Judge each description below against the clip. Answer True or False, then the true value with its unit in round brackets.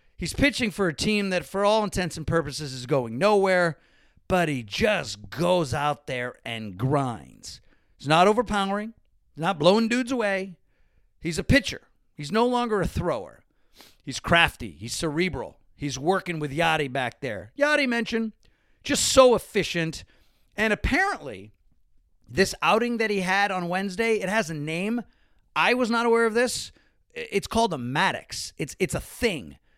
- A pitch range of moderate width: False (6.8 semitones)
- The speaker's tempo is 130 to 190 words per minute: True (160 wpm)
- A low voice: False (185 Hz)